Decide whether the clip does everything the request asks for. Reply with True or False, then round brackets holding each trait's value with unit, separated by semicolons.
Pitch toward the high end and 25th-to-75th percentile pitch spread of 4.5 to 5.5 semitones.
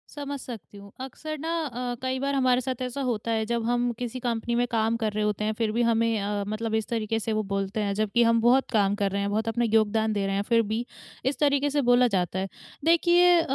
False (230 Hz; 3.1 semitones)